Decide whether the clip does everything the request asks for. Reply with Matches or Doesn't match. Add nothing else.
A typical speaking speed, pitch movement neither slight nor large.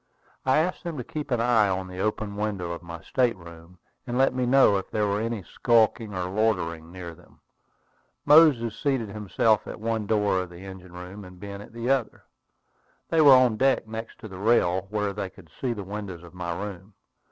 Doesn't match